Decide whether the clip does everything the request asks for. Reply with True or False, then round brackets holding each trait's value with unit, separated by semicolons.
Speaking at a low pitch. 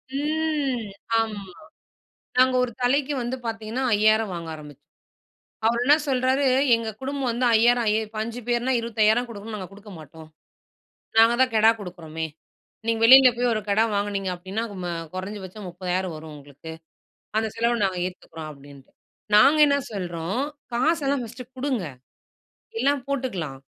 False (220 Hz)